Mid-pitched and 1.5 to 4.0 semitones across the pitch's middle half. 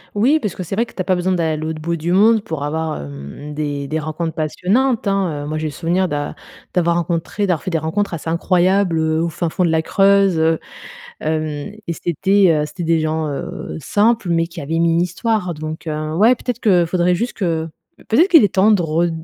Yes: medium, 170 Hz; average, 3.6 semitones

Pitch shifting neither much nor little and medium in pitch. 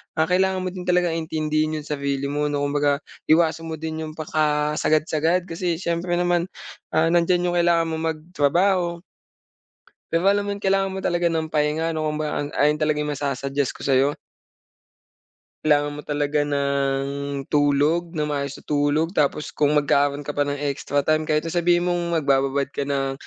Yes: average, 3.0 semitones; medium, 155 Hz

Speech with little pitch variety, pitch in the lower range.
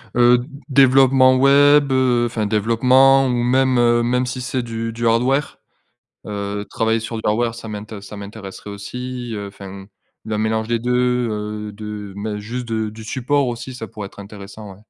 No: average, 3.1 semitones; low, 115 Hz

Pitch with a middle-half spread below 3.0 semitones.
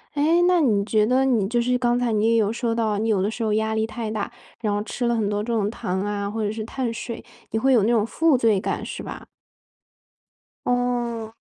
Yes: narrow, 2.5 semitones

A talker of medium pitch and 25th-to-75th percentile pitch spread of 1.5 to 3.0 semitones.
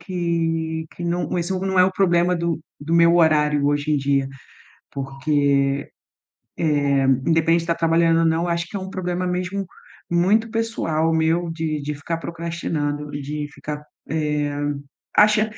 Yes: medium, 165 Hz; average, 2.7 semitones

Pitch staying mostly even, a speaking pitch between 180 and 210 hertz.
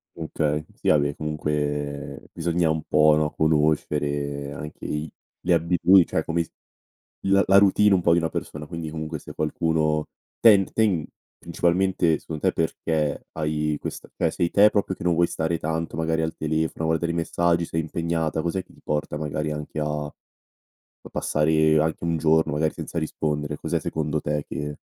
No: narrow, 1.8 semitones; very low, 80 Hz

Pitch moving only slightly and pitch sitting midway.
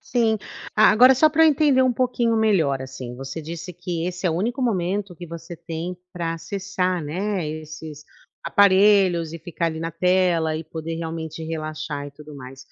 No: average, 4.2 semitones; medium, 170 Hz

